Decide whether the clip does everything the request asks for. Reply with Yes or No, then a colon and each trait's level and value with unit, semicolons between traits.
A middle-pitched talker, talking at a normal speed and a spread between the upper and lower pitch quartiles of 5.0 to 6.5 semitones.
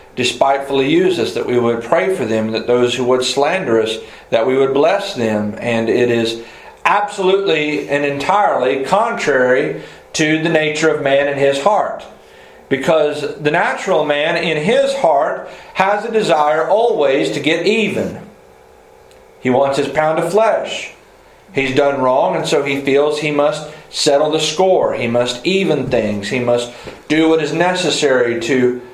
Yes: medium, 145 Hz; average, 160 wpm; average, 5.3 semitones